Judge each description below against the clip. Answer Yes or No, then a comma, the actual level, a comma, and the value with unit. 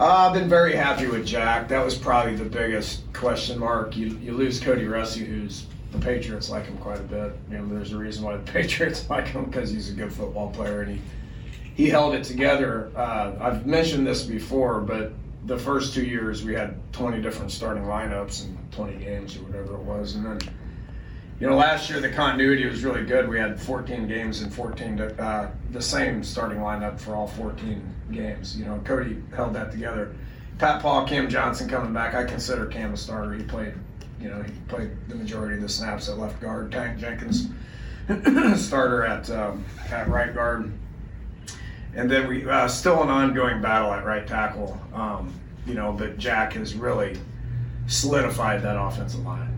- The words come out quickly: No, average, 190 wpm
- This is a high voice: No, low, 110 Hz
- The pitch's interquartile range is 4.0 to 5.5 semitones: No, average, 2.9 semitones